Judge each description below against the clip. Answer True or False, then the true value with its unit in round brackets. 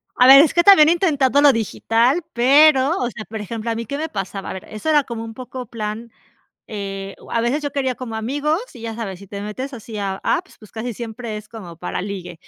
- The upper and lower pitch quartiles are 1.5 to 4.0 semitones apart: False (4.7 semitones)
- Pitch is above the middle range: True (230 Hz)